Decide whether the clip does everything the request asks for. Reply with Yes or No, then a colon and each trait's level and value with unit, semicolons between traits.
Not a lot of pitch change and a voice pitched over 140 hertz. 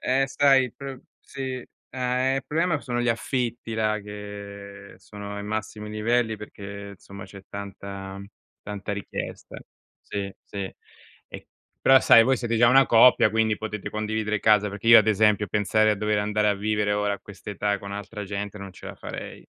No: narrow, 2.2 semitones; low, 105 Hz